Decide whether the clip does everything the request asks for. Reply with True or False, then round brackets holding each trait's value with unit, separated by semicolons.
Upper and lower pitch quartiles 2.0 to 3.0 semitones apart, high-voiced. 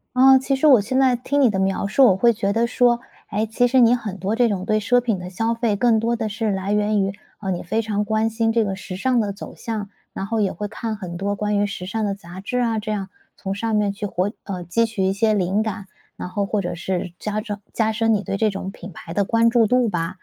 True (2.7 semitones; 210 Hz)